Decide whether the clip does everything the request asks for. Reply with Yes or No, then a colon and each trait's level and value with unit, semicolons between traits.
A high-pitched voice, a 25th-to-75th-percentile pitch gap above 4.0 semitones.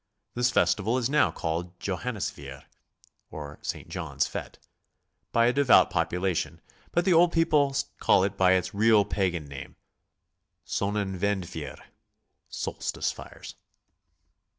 No: low, 100 Hz; wide, 5.5 semitones